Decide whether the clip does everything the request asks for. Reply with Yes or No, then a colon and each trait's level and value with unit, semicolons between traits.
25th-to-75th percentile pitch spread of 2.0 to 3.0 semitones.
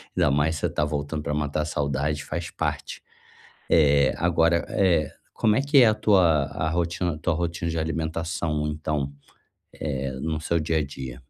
Yes: narrow, 2.5 semitones